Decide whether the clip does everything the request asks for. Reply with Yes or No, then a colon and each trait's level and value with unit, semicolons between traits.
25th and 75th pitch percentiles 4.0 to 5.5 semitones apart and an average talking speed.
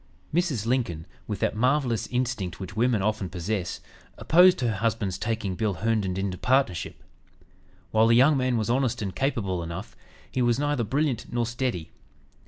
Yes: average, 4.8 semitones; average, 160 wpm